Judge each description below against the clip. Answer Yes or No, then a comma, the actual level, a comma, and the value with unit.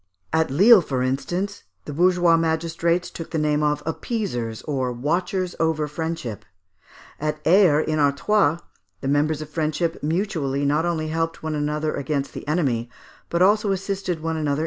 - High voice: No, medium, 160 Hz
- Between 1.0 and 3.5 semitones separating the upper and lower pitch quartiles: Yes, average, 2.9 semitones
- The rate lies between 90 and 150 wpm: No, average, 165 wpm